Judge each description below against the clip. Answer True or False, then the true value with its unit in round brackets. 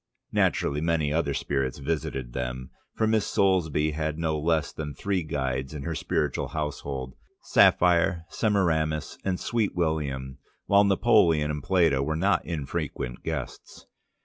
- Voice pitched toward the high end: False (80 Hz)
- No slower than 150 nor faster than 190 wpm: False (135 wpm)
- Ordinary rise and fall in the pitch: True (3.7 semitones)